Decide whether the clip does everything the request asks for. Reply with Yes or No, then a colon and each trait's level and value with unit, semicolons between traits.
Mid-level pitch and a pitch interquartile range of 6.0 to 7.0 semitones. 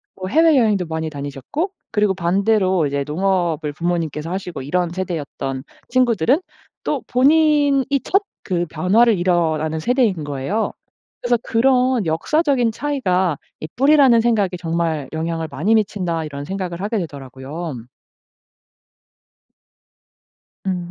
Yes: medium, 180 Hz; wide, 6.5 semitones